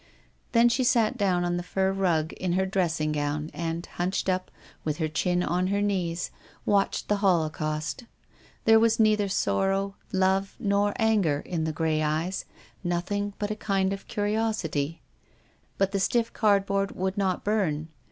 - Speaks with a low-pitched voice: No, high, 190 Hz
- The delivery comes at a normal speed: Yes, average, 160 wpm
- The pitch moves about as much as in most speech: Yes, average, 3.6 semitones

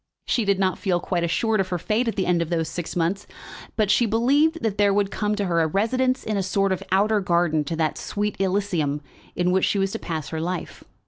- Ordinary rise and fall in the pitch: Yes, average, 3.4 semitones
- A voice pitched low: No, high, 195 Hz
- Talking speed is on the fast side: Yes, fast, 245 wpm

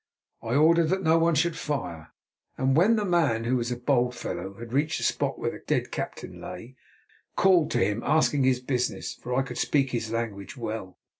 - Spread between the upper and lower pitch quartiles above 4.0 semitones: Yes, wide, 5.6 semitones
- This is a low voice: Yes, low, 130 Hz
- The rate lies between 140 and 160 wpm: No, fast, 205 wpm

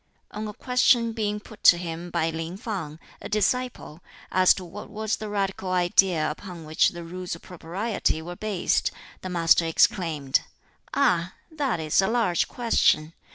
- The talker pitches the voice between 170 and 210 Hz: Yes, medium, 185 Hz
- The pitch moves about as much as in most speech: Yes, average, 4.3 semitones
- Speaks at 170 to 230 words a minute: No, average, 160 wpm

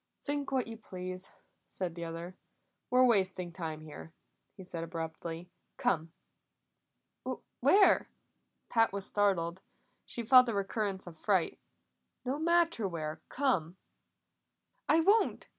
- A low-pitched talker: No, high, 190 Hz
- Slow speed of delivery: Yes, slow, 120 wpm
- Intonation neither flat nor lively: No, wide, 6.5 semitones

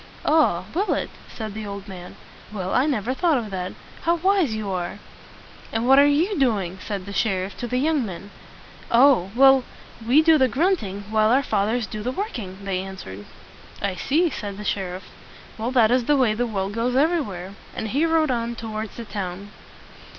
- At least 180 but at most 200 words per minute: Yes, average, 190 wpm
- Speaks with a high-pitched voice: Yes, high, 225 Hz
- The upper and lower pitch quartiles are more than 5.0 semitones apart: Yes, wide, 5.6 semitones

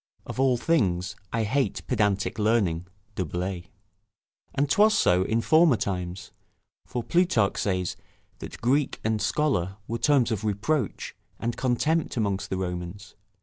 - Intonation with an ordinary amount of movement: No, wide, 5.7 semitones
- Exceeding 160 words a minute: No, average, 140 wpm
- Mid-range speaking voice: No, low, 110 Hz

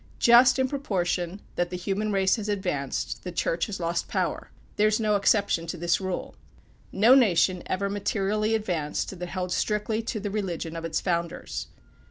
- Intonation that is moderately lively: Yes, average, 3.4 semitones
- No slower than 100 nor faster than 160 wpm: No, average, 175 wpm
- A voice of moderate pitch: No, high, 195 Hz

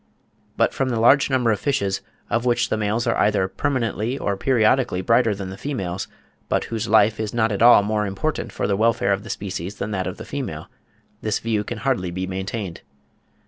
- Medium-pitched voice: No, low, 110 Hz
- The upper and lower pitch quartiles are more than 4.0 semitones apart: No, average, 3.3 semitones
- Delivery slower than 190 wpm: No, fast, 205 wpm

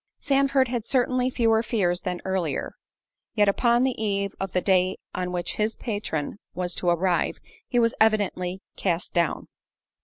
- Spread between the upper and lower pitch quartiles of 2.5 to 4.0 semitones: No, average, 4.6 semitones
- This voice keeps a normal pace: Yes, average, 155 wpm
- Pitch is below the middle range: No, high, 200 Hz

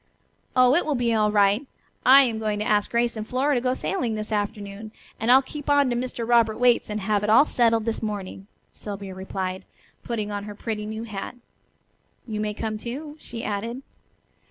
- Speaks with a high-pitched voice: Yes, high, 220 Hz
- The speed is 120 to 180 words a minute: No, average, 200 wpm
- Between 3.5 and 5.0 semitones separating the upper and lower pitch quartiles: No, average, 2.7 semitones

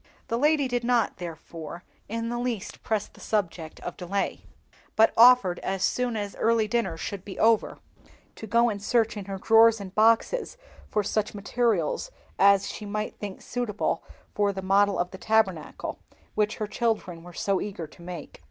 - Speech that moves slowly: No, average, 175 wpm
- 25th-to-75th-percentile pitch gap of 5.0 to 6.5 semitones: No, average, 3.3 semitones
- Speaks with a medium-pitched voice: No, high, 210 Hz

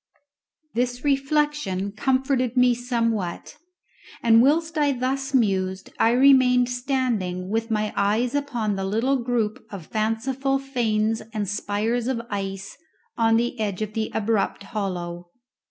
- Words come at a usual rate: No, slow, 130 wpm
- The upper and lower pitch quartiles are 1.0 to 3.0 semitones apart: No, average, 4.0 semitones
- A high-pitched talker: Yes, high, 230 Hz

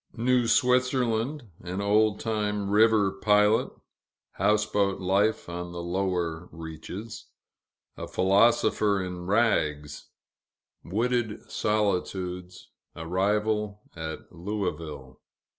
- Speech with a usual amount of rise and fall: Yes, average, 3.4 semitones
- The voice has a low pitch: Yes, low, 100 Hz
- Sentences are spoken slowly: Yes, slow, 85 wpm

